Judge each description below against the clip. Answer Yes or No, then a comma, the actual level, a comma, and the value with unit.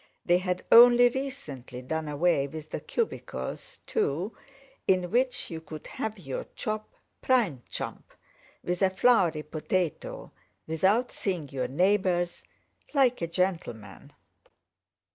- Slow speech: Yes, slow, 120 wpm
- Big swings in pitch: Yes, wide, 5.8 semitones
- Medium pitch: Yes, medium, 180 Hz